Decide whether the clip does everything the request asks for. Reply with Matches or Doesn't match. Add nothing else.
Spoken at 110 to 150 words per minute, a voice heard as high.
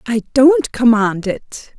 Matches